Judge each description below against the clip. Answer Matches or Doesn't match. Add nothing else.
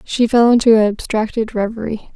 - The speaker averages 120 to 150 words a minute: Matches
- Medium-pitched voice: Doesn't match